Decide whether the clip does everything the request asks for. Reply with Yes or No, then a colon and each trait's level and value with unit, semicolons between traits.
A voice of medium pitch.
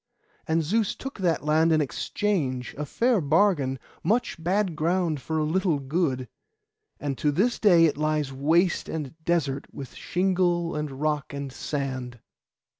Yes: medium, 155 Hz